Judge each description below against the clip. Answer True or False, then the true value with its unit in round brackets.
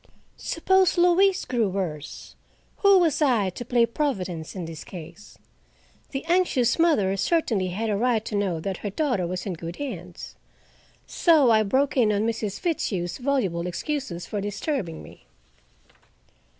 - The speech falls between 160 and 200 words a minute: False (150 wpm)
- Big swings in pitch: True (7.7 semitones)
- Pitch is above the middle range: True (215 Hz)